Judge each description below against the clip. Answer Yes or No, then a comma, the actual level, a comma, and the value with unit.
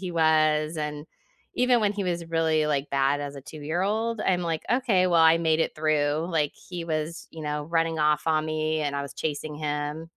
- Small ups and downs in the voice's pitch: Yes, narrow, 2.1 semitones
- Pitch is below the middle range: No, medium, 155 Hz